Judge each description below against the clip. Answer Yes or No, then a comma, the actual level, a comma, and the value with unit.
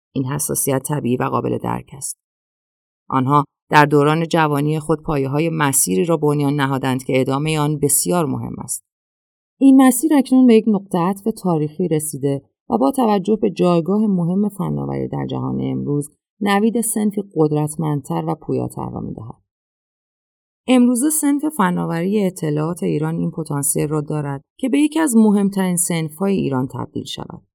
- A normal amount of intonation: No, wide, 6.8 semitones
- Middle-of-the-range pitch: Yes, medium, 155 Hz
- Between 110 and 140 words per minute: No, average, 150 wpm